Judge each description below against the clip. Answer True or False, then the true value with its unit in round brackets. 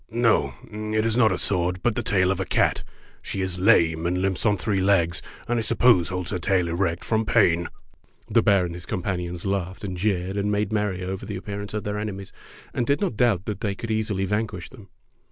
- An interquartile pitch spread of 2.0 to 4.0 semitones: True (3.0 semitones)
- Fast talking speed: True (220 wpm)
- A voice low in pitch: True (100 Hz)